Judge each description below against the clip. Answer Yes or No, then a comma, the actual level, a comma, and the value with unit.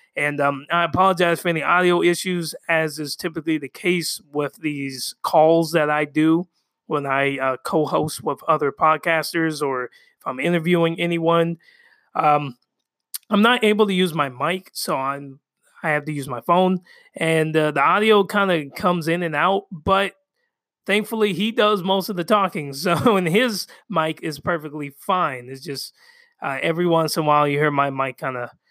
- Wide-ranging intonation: No, average, 3.9 semitones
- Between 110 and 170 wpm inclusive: No, average, 180 wpm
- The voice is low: No, medium, 165 Hz